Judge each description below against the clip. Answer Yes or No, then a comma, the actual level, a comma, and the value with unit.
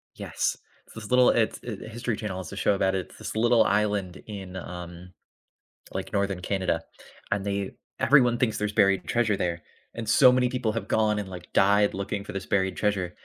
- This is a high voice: No, low, 100 Hz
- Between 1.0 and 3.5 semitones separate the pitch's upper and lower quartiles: Yes, average, 2.7 semitones